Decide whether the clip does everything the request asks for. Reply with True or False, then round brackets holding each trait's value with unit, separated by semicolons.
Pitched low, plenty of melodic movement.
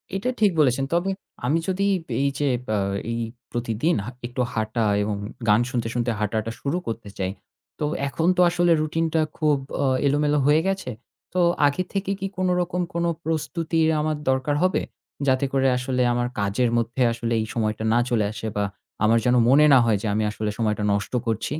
True (130 Hz; 6.0 semitones)